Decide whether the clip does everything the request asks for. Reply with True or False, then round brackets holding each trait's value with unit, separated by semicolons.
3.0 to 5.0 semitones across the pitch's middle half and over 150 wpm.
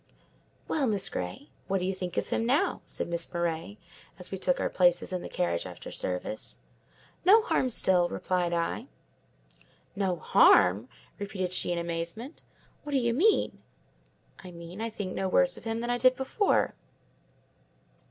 False (5.4 semitones; 165 wpm)